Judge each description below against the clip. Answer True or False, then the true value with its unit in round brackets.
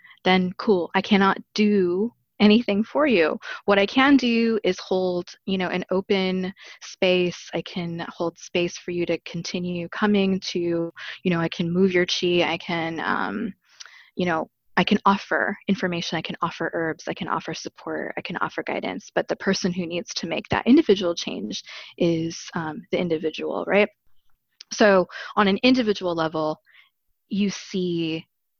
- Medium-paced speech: True (165 wpm)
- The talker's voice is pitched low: False (185 Hz)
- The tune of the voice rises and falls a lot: False (3.2 semitones)